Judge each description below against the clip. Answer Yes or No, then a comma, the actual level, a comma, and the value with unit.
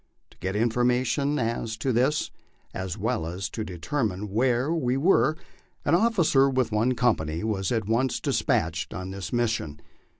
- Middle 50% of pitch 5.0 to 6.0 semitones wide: Yes, average, 5.3 semitones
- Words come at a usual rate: Yes, average, 155 wpm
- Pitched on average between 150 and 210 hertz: No, low, 115 Hz